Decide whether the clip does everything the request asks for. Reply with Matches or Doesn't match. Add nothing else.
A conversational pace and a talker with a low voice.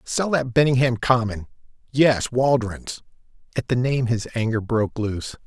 Doesn't match